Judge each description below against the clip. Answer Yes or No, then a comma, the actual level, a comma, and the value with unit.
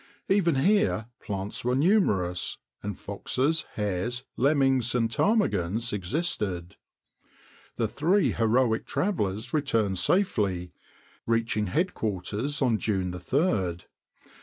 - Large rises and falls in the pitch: Yes, wide, 6.9 semitones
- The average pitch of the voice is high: No, low, 115 Hz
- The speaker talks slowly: Yes, slow, 95 wpm